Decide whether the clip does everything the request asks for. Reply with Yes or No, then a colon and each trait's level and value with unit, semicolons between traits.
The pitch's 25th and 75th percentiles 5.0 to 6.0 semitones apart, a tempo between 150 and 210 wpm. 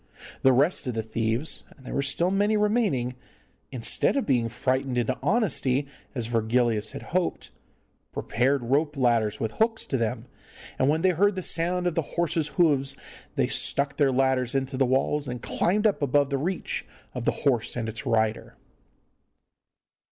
Yes: wide, 5.4 semitones; average, 170 wpm